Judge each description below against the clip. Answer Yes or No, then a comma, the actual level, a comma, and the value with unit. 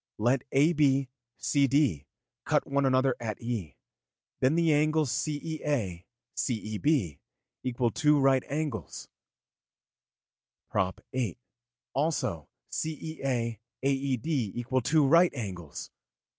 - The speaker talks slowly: Yes, slow, 95 wpm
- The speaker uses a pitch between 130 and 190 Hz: Yes, low, 135 Hz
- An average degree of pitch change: Yes, average, 4.4 semitones